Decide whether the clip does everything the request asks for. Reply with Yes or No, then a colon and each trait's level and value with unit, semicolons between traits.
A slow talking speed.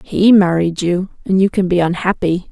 No: average, 165 wpm